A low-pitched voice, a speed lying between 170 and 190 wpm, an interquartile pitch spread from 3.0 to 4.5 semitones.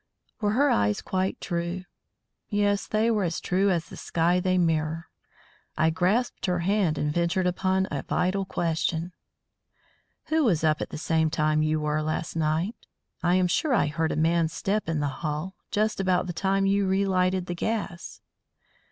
No: medium, 180 Hz; average, 175 wpm; average, 3.4 semitones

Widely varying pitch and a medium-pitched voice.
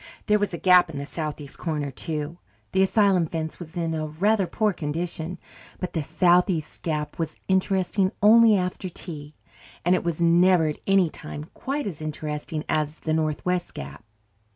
No: average, 3.2 semitones; medium, 170 Hz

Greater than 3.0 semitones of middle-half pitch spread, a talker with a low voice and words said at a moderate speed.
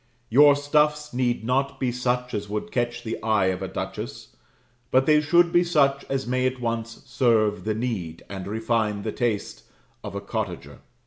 Yes: average, 4.0 semitones; low, 120 Hz; average, 180 wpm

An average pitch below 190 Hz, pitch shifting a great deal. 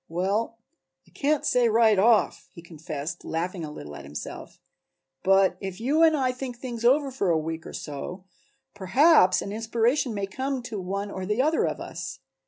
No: high, 205 Hz; wide, 5.8 semitones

